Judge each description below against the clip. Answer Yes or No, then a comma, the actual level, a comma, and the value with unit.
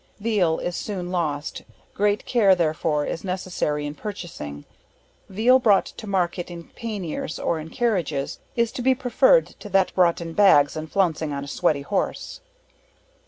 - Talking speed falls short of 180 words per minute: Yes, average, 160 wpm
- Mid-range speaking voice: Yes, medium, 180 Hz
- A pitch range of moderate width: Yes, average, 4.8 semitones